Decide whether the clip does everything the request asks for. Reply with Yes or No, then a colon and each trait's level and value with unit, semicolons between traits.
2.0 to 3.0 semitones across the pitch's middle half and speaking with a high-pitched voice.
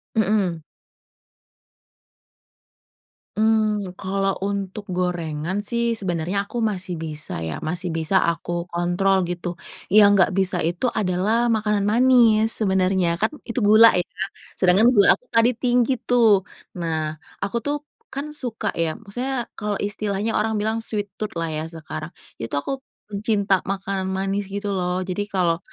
No: average, 3.5 semitones; high, 200 Hz